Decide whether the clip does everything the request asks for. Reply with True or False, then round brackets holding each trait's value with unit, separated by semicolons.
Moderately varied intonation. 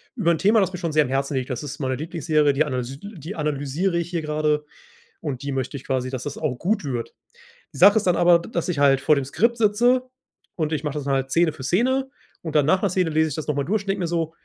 True (4.6 semitones)